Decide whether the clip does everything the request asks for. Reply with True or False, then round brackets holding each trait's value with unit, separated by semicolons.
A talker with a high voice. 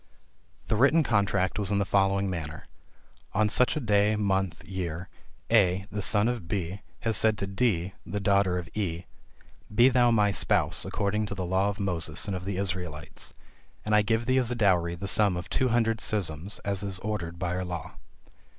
False (100 Hz)